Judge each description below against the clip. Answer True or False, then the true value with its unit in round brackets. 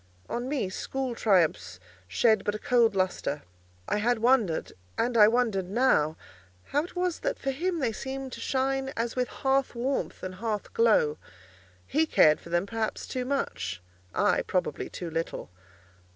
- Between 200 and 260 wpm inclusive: False (155 wpm)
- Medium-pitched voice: False (230 Hz)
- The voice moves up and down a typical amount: False (6.2 semitones)